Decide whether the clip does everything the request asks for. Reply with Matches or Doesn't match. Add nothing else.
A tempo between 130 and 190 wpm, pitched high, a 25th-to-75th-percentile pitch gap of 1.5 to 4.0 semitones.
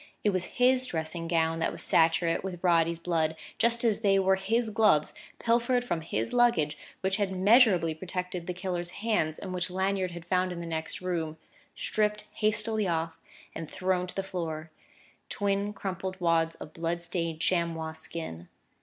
Doesn't match